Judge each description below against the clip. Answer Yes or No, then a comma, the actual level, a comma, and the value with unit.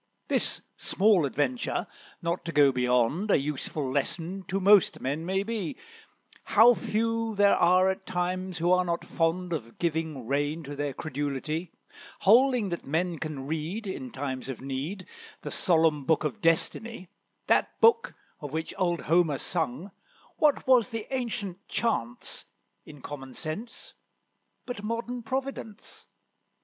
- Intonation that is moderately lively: No, wide, 6.1 semitones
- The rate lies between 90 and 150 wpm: Yes, average, 140 wpm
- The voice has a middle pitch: Yes, medium, 175 Hz